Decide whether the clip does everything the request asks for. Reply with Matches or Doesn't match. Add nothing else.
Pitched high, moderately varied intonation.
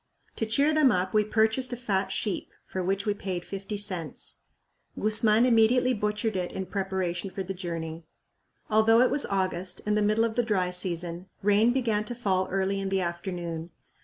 Matches